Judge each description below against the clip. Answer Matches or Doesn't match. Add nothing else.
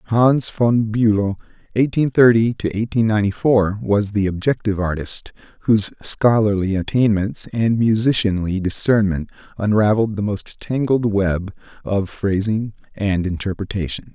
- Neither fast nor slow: Doesn't match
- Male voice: Matches